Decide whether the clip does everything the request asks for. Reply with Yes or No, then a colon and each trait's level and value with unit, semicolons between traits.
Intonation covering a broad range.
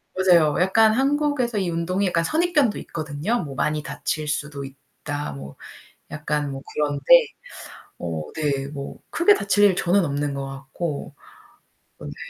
Yes: wide, 6.0 semitones